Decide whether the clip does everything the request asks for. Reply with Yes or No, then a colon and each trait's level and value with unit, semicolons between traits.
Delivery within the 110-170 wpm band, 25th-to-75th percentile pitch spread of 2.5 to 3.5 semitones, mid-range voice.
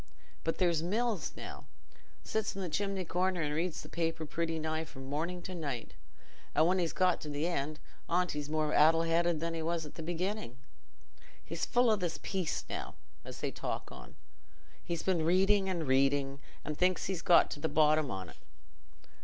No: average, 185 wpm; average, 3.0 semitones; medium, 165 Hz